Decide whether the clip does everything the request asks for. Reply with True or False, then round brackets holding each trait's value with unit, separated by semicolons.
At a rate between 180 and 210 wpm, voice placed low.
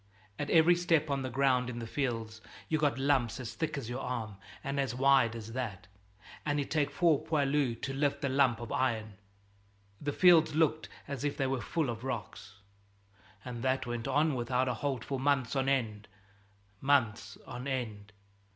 True (185 wpm; 130 Hz)